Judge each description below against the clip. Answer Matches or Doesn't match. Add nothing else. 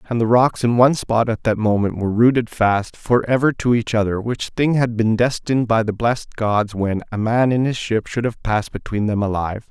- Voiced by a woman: Doesn't match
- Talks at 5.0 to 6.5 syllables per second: Matches